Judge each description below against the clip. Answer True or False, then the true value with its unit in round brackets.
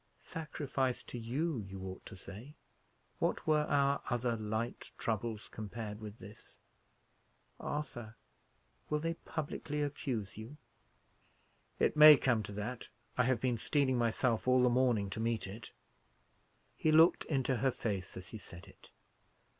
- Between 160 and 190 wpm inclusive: False (145 wpm)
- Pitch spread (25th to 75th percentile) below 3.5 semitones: False (4.5 semitones)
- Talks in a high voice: False (120 Hz)